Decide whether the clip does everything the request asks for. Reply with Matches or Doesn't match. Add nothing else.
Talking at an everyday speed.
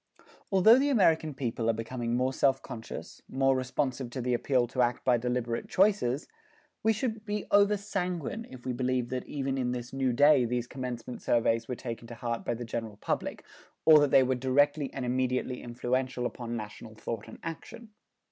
Matches